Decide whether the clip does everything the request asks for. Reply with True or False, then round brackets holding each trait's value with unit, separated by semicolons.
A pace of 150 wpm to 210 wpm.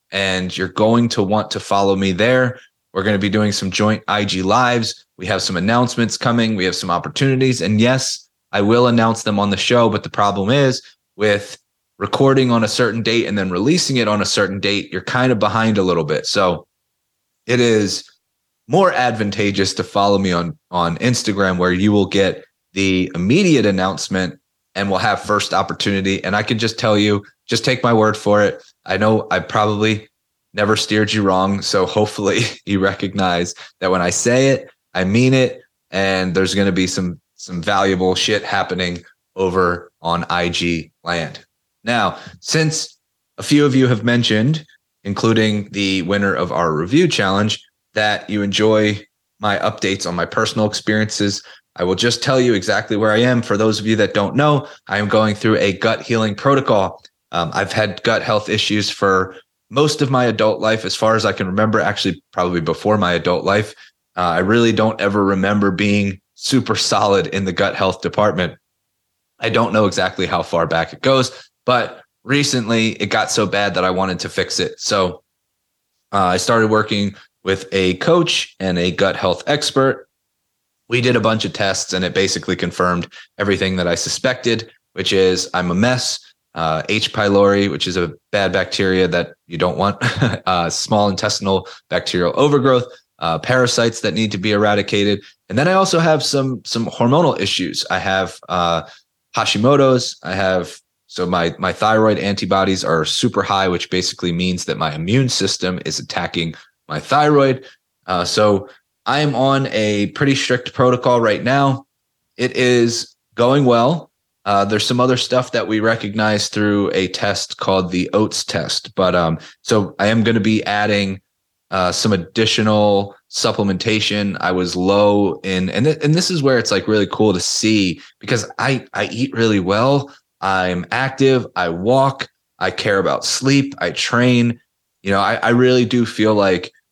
True (180 wpm)